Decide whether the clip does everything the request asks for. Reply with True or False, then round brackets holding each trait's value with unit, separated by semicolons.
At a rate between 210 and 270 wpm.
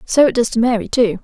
False (290 wpm)